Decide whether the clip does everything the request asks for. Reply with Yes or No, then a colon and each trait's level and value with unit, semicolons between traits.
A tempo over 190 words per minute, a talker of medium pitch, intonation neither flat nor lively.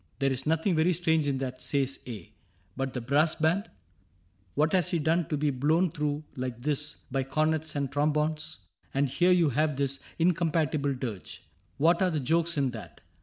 Yes: average, 200 wpm; medium, 150 Hz; average, 3.1 semitones